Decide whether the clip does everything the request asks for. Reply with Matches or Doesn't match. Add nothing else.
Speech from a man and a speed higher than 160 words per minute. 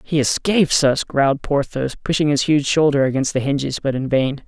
Matches